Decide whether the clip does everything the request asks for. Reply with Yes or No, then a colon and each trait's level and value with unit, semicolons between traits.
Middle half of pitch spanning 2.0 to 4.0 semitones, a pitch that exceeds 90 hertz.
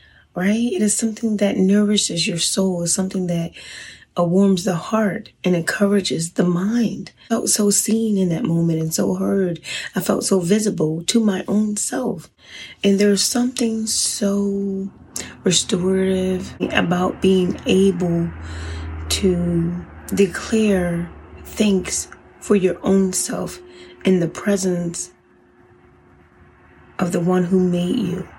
Yes: average, 2.8 semitones; high, 190 Hz